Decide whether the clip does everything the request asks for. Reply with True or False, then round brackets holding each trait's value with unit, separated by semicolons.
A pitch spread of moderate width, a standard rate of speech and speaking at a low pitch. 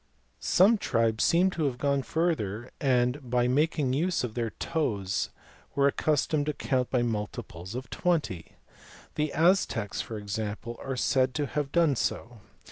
True (4.9 semitones; 150 wpm; 130 Hz)